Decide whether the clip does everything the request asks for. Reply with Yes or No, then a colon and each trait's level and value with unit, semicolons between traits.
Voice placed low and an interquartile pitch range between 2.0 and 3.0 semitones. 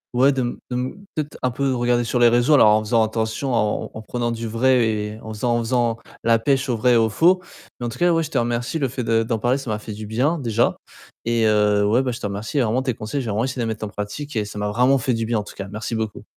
Yes: low, 115 Hz; average, 2.7 semitones